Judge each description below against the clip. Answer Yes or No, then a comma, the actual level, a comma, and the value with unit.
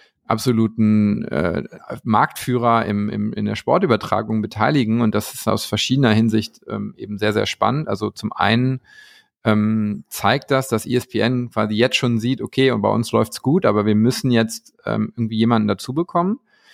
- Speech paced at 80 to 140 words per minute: No, average, 170 wpm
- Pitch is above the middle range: No, low, 115 Hz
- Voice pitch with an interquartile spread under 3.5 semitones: Yes, average, 3.0 semitones